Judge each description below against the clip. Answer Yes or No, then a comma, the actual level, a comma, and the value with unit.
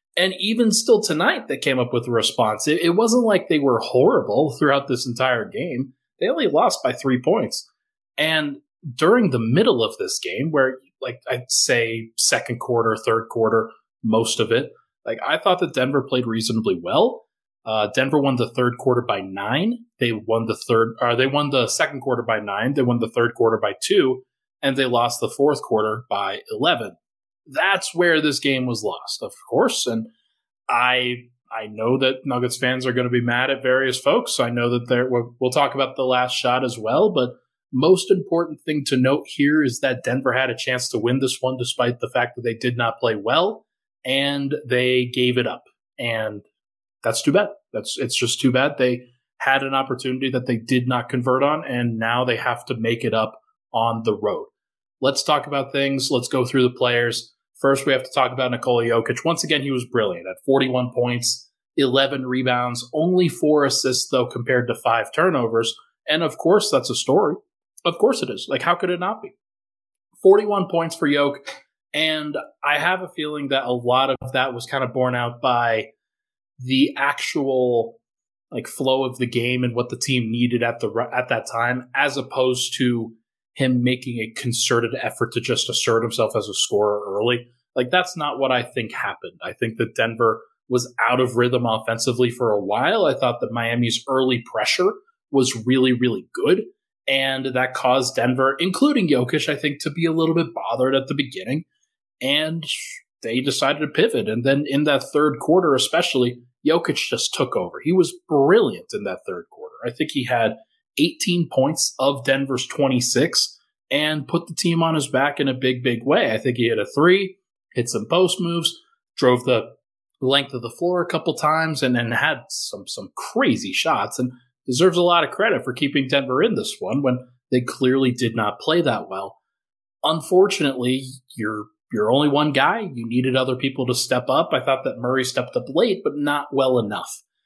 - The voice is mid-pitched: No, low, 130 Hz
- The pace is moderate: Yes, average, 195 wpm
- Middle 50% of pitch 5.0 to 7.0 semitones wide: No, average, 3.6 semitones